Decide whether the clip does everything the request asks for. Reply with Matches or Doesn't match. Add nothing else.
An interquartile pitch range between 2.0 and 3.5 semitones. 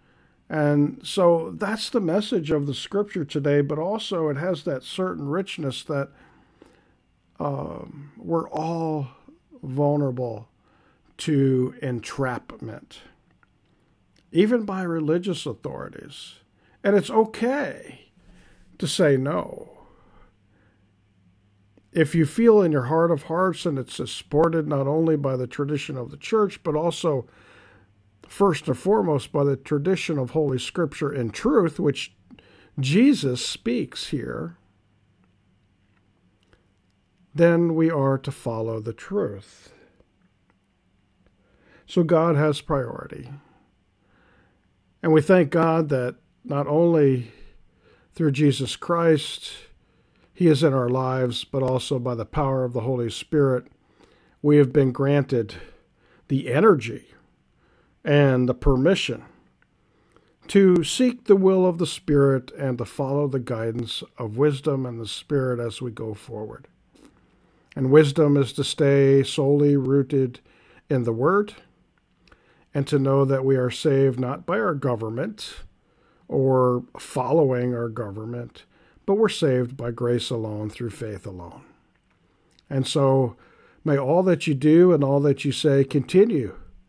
Doesn't match